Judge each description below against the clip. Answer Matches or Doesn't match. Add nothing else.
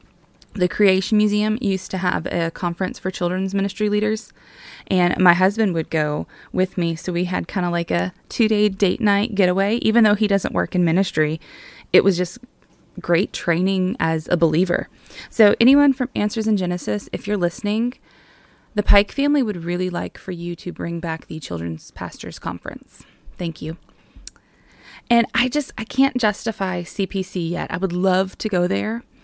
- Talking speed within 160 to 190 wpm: Matches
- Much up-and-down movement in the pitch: Doesn't match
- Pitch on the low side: Doesn't match